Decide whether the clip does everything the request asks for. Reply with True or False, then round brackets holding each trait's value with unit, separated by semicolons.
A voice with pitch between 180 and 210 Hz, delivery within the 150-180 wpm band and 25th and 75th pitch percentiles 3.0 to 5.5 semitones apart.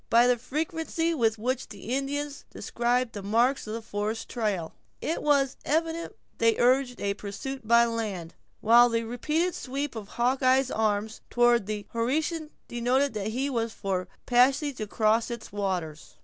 False (240 Hz; 160 wpm; 3.9 semitones)